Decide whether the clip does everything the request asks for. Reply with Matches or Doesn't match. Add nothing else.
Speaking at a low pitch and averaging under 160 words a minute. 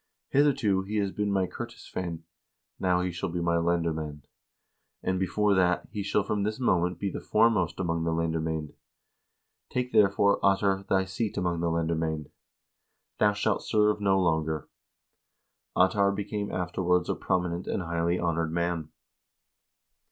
Matches